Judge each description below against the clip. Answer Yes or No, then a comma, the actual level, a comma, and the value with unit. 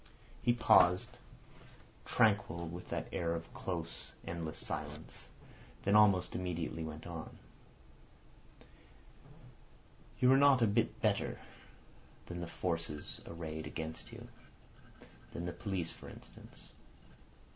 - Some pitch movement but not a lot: Yes, average, 3.3 semitones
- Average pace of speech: No, slow, 105 wpm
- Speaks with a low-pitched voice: Yes, very low, 85 Hz